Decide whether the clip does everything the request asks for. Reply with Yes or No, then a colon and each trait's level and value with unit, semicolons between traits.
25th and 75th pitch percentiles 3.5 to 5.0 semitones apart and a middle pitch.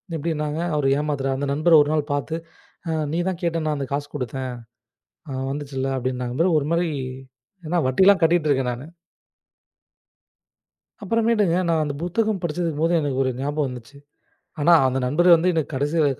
Yes: average, 3.8 semitones; medium, 150 Hz